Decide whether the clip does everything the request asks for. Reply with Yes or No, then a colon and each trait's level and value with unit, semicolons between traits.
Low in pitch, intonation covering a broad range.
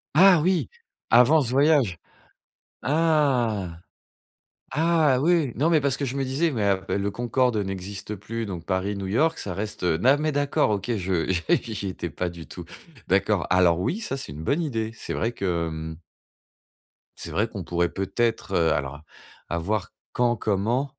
Yes: low, 110 Hz; wide, 7.0 semitones